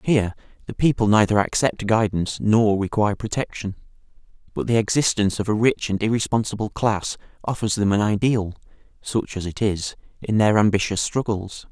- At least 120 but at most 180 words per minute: Yes, average, 155 wpm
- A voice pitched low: Yes, low, 105 Hz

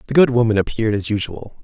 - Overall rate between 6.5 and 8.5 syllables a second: Yes, 7.1 syllables/s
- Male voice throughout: Yes, male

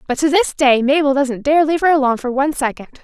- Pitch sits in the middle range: No, very high, 280 Hz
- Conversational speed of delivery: No, fast, 255 wpm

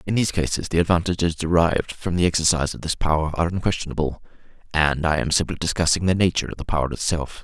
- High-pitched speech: No, very low, 85 Hz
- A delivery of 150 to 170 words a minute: No, average, 200 wpm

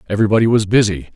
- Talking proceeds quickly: No, average, 155 wpm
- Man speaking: Yes, male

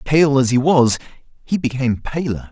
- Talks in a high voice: No, low, 130 Hz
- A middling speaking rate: Yes, average, 165 wpm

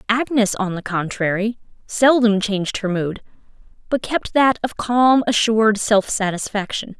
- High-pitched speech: Yes, high, 215 Hz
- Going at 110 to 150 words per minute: Yes, slow, 135 wpm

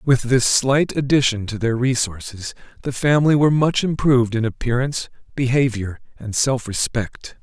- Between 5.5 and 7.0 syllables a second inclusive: No, 4.9 syllables/s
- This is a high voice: No, low, 125 Hz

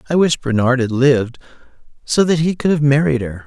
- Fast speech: Yes, fast, 210 wpm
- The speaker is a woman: No, male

